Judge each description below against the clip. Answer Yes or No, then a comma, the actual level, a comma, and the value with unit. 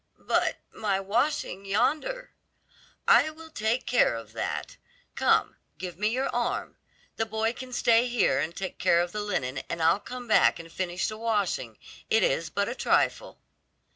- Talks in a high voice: Yes, high, 215 Hz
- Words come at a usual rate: Yes, average, 170 wpm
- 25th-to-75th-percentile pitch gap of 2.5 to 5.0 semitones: No, wide, 5.5 semitones